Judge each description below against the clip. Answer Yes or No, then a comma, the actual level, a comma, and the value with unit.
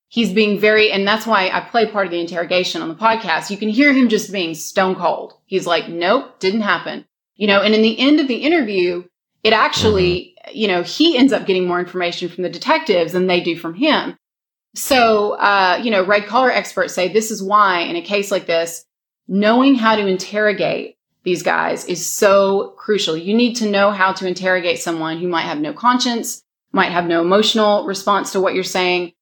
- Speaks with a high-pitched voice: Yes, high, 200 Hz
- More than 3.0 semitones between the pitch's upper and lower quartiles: Yes, average, 3.6 semitones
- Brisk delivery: Yes, fast, 210 wpm